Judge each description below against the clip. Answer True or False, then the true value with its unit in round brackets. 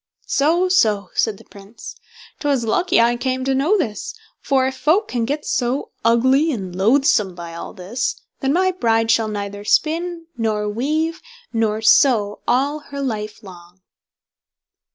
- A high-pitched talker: True (240 Hz)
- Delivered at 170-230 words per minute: False (155 wpm)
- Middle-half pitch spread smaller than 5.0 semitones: False (5.5 semitones)